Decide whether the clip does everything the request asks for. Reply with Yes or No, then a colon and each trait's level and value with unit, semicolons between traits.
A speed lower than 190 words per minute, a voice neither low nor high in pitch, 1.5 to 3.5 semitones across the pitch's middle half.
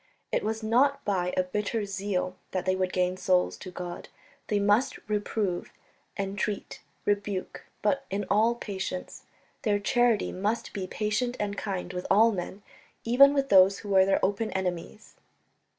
No: average, 155 wpm; high, 200 Hz; narrow, 2.6 semitones